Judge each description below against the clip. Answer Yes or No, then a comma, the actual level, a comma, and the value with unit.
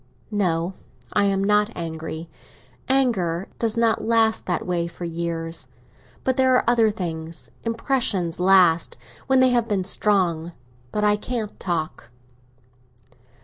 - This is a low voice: No, high, 195 Hz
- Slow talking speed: Yes, slow, 130 wpm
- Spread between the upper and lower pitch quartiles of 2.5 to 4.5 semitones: No, average, 5.1 semitones